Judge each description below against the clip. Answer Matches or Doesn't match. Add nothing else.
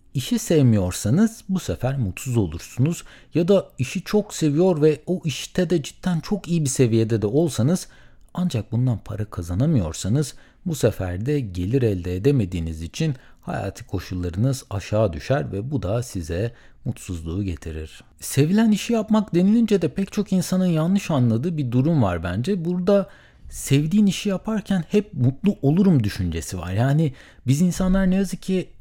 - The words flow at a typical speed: Doesn't match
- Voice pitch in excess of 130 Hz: Matches